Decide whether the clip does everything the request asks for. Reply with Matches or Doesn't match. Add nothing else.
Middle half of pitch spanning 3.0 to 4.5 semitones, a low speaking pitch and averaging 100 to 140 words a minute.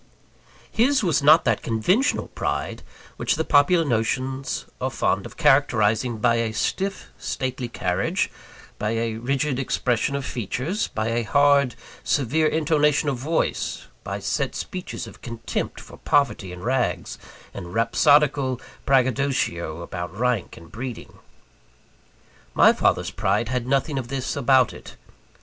Matches